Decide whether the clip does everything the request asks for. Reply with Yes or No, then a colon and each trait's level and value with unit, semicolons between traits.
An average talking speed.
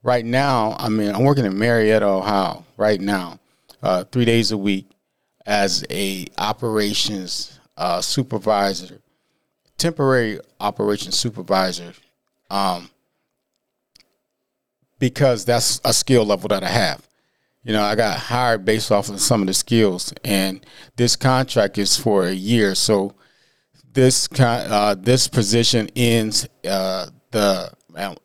No: slow, 130 wpm